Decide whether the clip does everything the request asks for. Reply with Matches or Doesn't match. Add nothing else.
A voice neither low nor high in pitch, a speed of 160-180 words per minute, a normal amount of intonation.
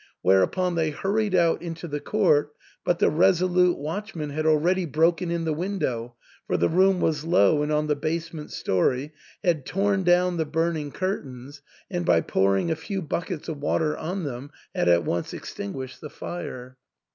Matches